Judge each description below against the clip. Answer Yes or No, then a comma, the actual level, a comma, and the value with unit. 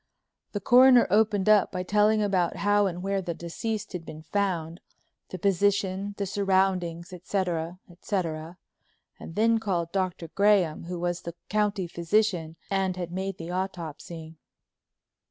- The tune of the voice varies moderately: Yes, average, 3.0 semitones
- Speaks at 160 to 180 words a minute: No, average, 140 wpm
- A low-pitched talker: No, medium, 185 Hz